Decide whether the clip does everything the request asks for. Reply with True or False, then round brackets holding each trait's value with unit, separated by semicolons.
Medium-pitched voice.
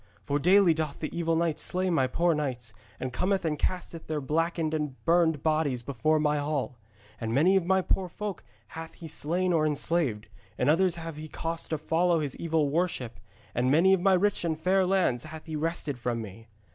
True (160 Hz)